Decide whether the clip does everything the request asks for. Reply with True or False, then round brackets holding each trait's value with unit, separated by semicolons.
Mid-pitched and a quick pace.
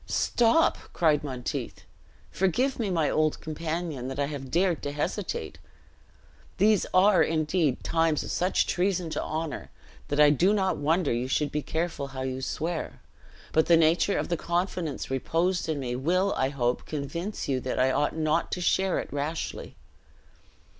False (160 Hz; 165 wpm)